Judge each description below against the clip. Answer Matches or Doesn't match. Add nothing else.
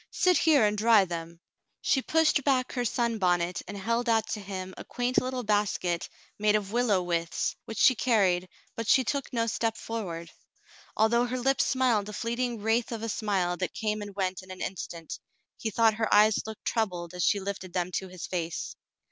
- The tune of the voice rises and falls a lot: Doesn't match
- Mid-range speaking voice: Doesn't match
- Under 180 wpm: Doesn't match